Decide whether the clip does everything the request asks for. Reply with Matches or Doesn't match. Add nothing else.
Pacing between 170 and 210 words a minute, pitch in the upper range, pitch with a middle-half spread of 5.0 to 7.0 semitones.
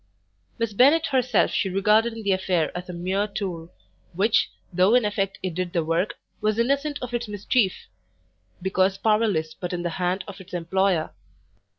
Doesn't match